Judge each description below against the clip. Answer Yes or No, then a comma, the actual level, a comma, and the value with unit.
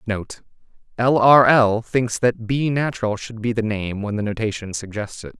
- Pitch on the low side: Yes, low, 115 Hz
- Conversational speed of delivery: Yes, average, 180 wpm